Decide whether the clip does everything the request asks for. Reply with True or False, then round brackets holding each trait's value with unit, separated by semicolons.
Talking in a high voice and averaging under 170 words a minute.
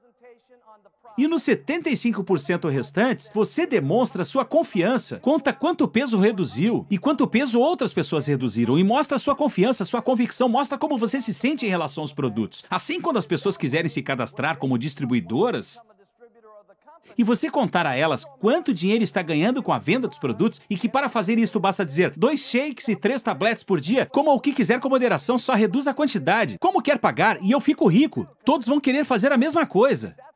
False (235 Hz; 185 wpm)